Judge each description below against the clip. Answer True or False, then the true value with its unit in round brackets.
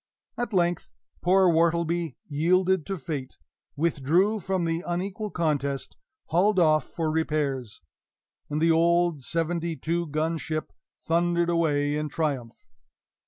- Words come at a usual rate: False (120 wpm)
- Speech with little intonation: True (2.3 semitones)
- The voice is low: False (165 Hz)